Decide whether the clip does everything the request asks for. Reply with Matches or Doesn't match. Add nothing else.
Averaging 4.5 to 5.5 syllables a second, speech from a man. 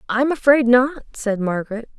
Doesn't match